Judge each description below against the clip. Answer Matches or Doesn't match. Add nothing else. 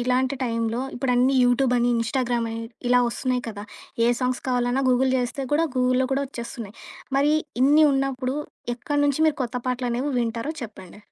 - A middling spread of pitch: Doesn't match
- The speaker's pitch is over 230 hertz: Matches